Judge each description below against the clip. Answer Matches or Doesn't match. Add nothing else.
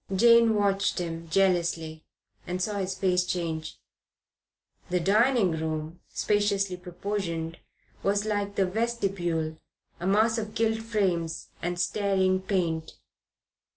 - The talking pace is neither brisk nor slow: Doesn't match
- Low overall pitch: Doesn't match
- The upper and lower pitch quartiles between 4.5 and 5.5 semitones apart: Doesn't match